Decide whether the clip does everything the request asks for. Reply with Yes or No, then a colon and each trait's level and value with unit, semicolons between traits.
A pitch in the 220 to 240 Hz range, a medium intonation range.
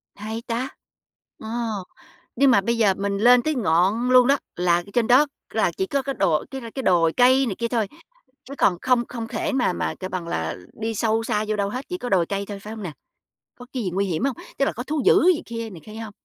Yes: high, 225 Hz; average, 4.2 semitones